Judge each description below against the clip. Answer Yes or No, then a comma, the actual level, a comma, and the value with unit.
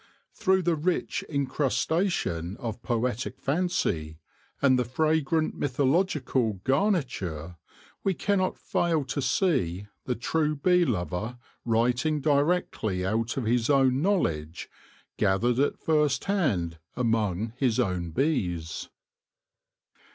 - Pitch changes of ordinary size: No, wide, 6.6 semitones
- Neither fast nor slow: No, slow, 105 wpm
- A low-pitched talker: Yes, low, 130 Hz